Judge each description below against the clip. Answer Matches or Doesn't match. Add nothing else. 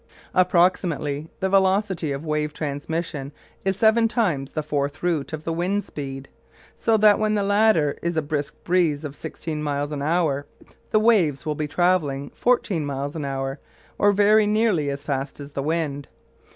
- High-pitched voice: Doesn't match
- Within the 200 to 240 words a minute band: Doesn't match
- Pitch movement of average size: Matches